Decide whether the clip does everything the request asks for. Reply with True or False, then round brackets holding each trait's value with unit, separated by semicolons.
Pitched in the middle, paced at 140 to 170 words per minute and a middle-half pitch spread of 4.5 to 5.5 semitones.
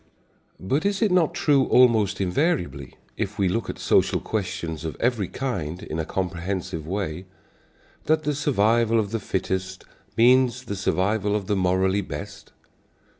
False (100 Hz; 150 wpm; 5.2 semitones)